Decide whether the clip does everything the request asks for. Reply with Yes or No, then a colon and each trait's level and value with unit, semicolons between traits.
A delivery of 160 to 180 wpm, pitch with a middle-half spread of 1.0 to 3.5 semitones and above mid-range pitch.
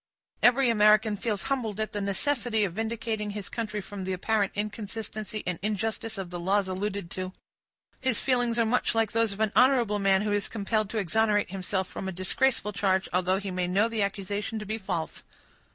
No: average, 195 wpm; narrow, 2.5 semitones; high, 210 Hz